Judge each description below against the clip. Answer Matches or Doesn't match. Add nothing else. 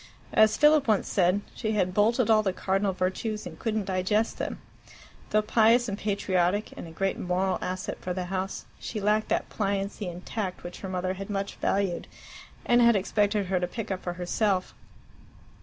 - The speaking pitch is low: Doesn't match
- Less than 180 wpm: Doesn't match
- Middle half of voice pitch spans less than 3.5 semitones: Matches